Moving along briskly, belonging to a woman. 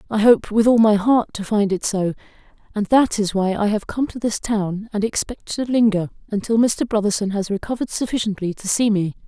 Yes: fast, 215 wpm; female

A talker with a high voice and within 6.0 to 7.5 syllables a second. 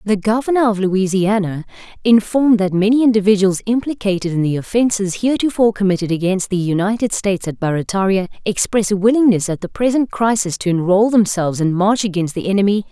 Yes: high, 200 Hz; 6.1 syllables/s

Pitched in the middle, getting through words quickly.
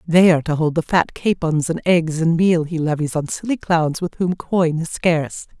Yes: medium, 165 Hz; fast, 225 wpm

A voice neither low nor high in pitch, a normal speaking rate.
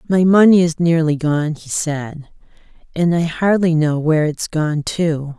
Yes: medium, 160 Hz; average, 165 wpm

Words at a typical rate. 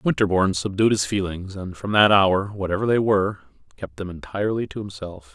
Yes: average, 180 wpm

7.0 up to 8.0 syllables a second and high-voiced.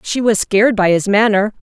No: 5.5 syllables/s; high, 210 Hz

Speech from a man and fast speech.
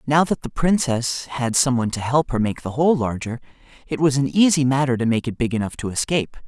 Yes: male; fast, 240 wpm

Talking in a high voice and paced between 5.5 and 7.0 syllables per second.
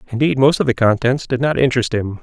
No: low, 130 Hz; 6.5 syllables/s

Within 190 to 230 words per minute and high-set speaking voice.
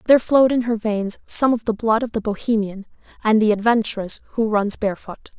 Yes: average, 200 wpm; high, 220 Hz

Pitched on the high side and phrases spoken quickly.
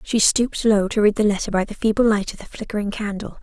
Yes: high, 210 Hz; fast, 265 wpm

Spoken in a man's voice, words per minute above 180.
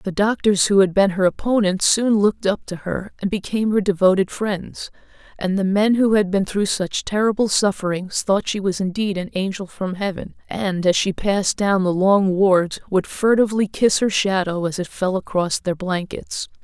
No: female; average, 195 wpm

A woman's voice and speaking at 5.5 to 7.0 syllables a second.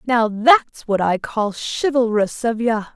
No: female; 4.1 syllables/s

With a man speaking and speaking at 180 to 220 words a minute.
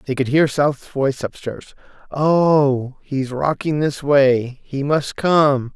No: male; average, 155 wpm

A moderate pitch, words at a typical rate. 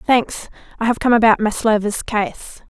No: high, 225 Hz; average, 155 wpm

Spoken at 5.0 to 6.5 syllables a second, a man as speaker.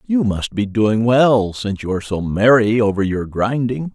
No: 4.7 syllables/s; male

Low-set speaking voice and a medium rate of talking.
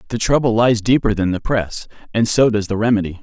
No: low, 110 Hz; fast, 225 wpm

